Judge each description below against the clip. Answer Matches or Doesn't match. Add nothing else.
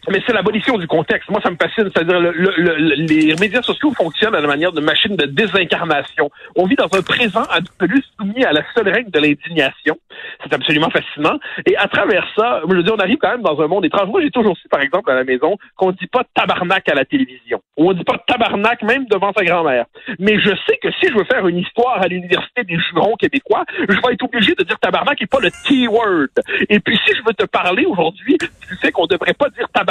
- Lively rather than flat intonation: Matches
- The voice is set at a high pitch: Matches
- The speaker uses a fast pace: Matches